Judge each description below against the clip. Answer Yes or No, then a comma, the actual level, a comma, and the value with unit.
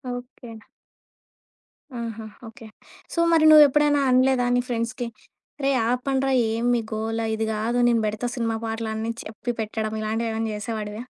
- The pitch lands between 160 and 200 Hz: No, high, 230 Hz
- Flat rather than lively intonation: Yes, narrow, 2.2 semitones